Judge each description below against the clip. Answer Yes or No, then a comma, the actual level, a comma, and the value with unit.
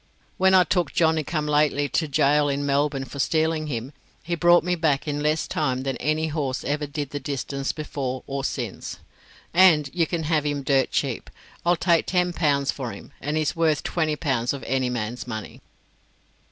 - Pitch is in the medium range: Yes, medium, 150 Hz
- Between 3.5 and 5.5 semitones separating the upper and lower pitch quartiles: No, average, 2.7 semitones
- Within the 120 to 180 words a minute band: No, average, 190 wpm